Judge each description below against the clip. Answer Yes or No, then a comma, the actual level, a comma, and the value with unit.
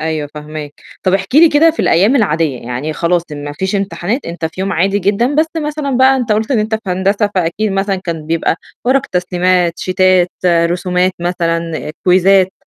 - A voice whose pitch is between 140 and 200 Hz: Yes, medium, 185 Hz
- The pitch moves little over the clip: No, average, 4.0 semitones